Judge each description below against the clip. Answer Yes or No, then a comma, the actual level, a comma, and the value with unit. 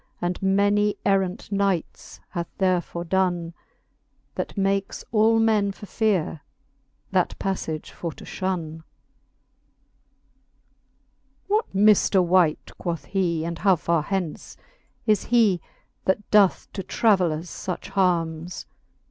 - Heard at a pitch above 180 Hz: Yes, high, 190 Hz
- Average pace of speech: No, slow, 115 wpm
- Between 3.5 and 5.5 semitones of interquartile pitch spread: No, average, 2.9 semitones